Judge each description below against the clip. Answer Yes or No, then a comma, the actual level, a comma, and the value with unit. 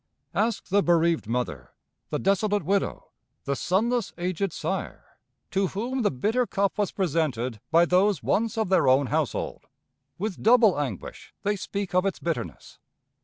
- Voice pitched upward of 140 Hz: Yes, high, 190 Hz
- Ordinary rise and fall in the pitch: Yes, average, 4.0 semitones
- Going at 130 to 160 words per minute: Yes, average, 150 wpm